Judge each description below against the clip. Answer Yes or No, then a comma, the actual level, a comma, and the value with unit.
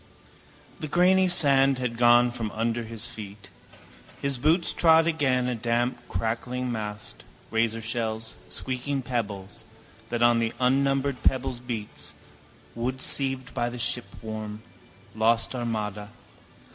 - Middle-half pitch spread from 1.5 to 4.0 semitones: Yes, average, 2.8 semitones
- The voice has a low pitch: Yes, low, 120 Hz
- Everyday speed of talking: No, slow, 120 wpm